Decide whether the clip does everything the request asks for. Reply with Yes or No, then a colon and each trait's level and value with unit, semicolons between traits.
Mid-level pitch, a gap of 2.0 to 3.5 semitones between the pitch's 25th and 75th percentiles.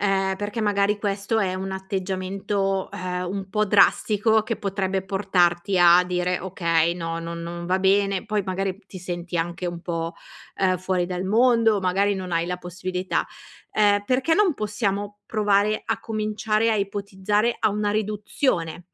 No: high, 195 Hz; narrow, 2.4 semitones